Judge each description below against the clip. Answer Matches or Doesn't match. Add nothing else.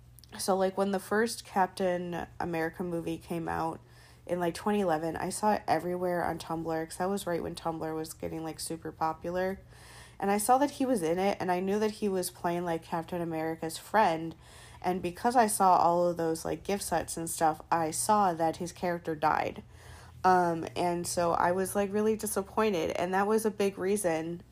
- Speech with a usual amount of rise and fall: Matches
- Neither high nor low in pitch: Matches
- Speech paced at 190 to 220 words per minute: Matches